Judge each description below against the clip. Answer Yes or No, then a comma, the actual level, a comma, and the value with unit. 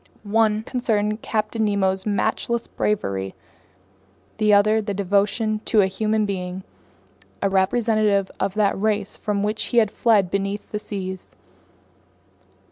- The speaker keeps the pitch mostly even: Yes, narrow, 1.7 semitones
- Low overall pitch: No, high, 210 Hz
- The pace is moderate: No, slow, 125 wpm